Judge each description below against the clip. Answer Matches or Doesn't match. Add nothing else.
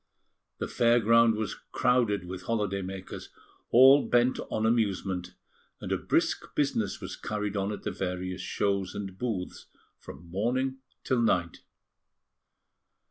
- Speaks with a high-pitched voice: Doesn't match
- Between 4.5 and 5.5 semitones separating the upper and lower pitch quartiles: Doesn't match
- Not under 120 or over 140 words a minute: Matches